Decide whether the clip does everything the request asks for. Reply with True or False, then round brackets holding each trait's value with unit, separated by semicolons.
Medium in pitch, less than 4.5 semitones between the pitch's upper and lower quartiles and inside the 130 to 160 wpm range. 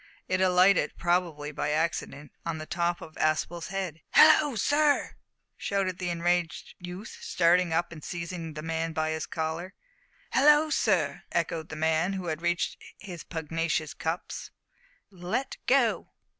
True (170 Hz; 2.5 semitones; 145 wpm)